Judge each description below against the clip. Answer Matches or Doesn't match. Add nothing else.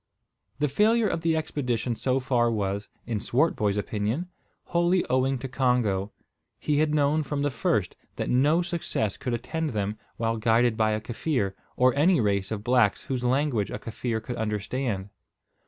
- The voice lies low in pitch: Matches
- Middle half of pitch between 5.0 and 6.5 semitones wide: Matches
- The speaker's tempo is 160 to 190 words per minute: Matches